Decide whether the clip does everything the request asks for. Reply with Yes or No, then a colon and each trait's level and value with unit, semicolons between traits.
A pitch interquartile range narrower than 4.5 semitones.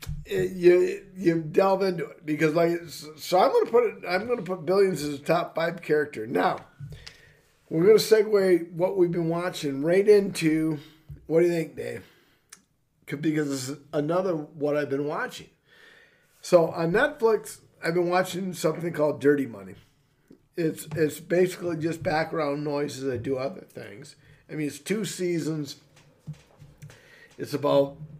Yes: average, 3.7 semitones